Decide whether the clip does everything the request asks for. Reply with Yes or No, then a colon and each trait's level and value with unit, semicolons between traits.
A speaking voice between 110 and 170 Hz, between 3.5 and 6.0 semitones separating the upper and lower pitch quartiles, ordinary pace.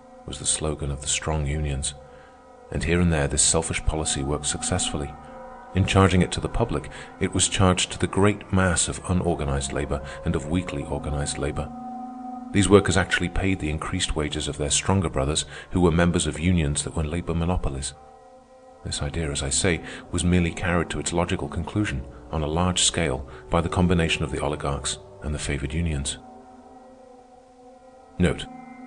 No: very low, 85 Hz; average, 4.5 semitones; average, 175 wpm